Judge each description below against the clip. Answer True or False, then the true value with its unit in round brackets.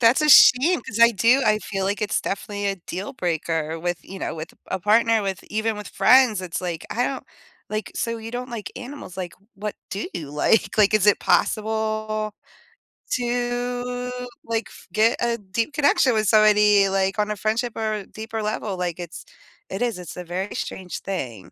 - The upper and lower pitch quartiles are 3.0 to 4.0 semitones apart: True (3.3 semitones)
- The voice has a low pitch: False (215 Hz)